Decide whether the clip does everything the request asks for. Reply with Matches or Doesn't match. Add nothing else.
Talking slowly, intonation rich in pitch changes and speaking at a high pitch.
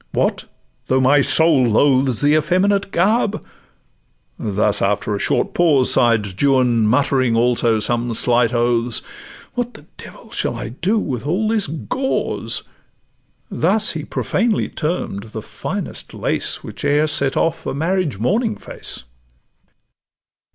Doesn't match